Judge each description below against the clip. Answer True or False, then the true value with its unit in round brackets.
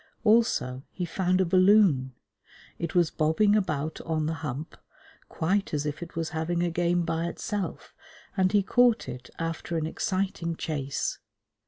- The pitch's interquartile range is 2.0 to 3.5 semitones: True (3.1 semitones)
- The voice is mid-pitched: True (170 Hz)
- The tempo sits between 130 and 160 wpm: True (155 wpm)